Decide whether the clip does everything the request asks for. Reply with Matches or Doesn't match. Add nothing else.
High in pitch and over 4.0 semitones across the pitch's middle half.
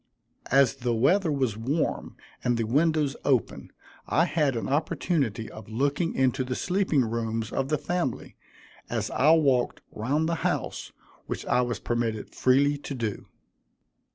Doesn't match